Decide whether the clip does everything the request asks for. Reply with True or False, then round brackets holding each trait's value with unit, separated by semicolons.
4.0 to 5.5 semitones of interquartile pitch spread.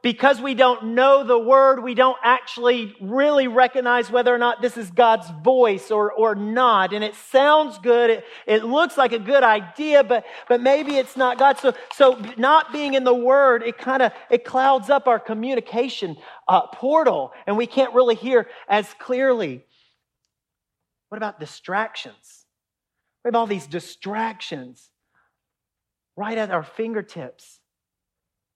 False (3.6 semitones)